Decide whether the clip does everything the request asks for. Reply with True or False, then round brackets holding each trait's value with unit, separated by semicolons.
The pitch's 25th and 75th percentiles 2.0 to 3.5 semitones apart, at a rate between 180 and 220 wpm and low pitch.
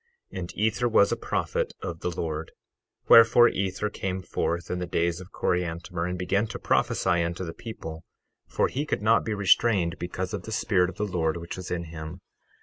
True (3.2 semitones; 200 wpm; 90 Hz)